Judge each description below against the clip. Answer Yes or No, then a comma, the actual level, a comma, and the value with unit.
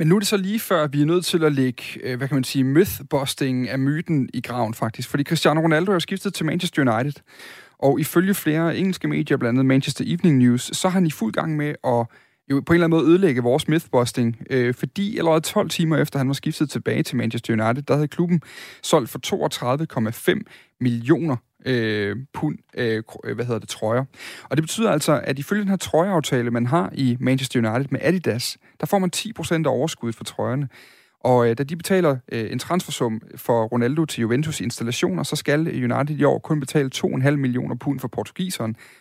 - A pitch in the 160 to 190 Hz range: No, medium, 140 Hz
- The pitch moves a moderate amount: Yes, average, 5.0 semitones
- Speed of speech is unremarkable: Yes, average, 205 wpm